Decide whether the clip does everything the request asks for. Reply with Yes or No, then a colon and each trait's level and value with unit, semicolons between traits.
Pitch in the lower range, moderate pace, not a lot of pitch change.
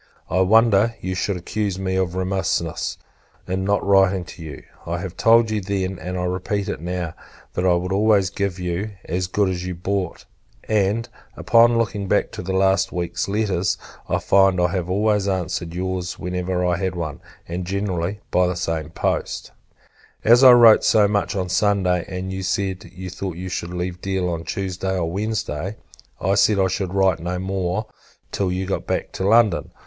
Yes: very low, 95 Hz; average, 185 wpm; narrow, 1.9 semitones